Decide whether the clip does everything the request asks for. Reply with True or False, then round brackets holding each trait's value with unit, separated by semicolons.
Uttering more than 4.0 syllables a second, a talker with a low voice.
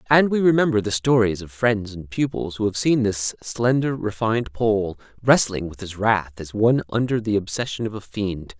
True (5.0 syllables/s; 110 Hz)